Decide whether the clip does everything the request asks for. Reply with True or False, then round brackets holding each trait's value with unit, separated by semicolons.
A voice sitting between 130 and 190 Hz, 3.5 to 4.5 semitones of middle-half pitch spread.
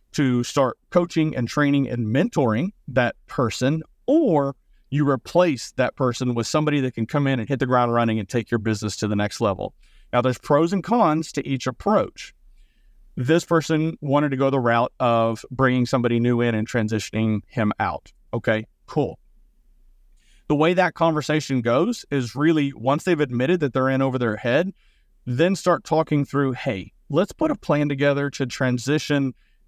True (135 Hz; 4.1 semitones)